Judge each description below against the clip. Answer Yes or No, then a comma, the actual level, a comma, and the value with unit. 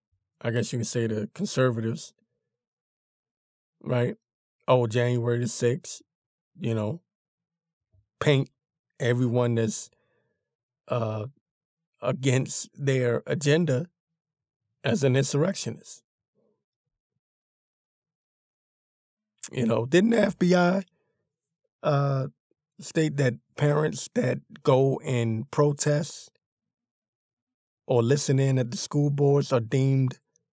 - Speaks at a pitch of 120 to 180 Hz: Yes, low, 135 Hz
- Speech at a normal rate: No, slow, 90 wpm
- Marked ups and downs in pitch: No, average, 4.6 semitones